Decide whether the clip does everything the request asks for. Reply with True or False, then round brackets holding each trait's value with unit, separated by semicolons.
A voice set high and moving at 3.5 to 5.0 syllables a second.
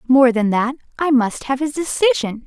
True (265 Hz; 4.8 syllables/s)